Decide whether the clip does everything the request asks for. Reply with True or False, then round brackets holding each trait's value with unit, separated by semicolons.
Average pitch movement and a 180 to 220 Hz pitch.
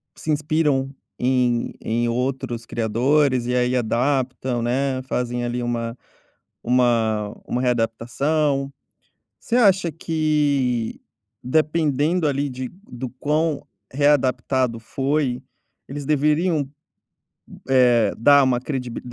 False (3.3 semitones; 130 Hz)